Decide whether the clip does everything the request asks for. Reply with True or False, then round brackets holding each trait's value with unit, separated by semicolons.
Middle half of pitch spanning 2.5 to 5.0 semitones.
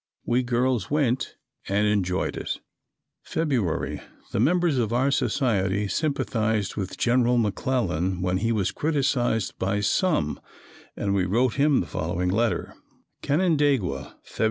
False (5.4 semitones)